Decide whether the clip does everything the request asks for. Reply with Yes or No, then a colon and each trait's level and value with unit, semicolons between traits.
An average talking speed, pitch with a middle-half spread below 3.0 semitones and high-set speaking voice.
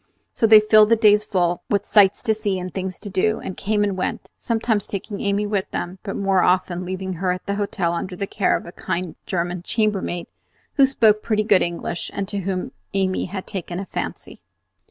No: fast, 210 wpm; narrow, 2.4 semitones; high, 195 Hz